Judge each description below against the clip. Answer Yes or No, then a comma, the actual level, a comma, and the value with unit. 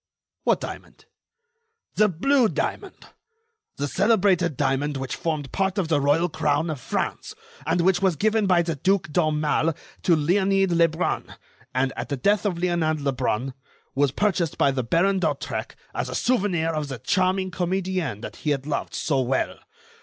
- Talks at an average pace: Yes, average, 160 wpm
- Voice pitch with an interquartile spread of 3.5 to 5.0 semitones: Yes, average, 4.7 semitones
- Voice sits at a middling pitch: Yes, medium, 165 Hz